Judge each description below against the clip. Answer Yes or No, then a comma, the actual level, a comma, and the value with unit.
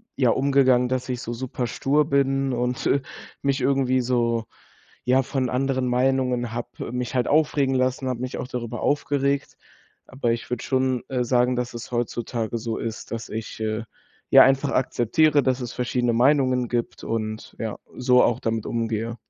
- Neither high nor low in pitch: No, low, 125 Hz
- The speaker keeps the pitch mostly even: Yes, narrow, 2.1 semitones